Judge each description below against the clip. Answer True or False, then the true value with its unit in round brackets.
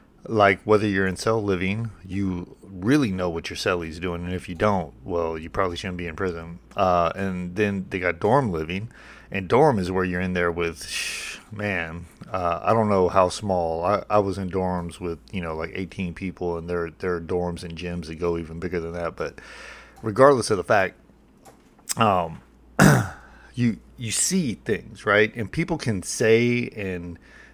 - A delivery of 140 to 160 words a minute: False (185 wpm)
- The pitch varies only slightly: False (3.1 semitones)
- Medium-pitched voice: False (90 Hz)